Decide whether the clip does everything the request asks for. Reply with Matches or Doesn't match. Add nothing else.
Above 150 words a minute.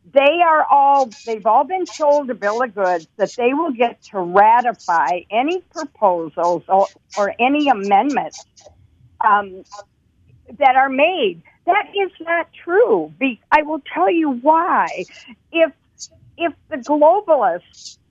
Doesn't match